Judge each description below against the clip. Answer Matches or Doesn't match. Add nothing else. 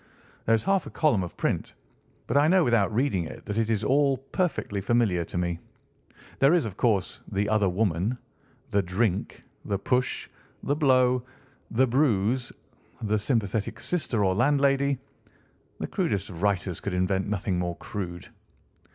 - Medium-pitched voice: Doesn't match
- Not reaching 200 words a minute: Matches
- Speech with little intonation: Doesn't match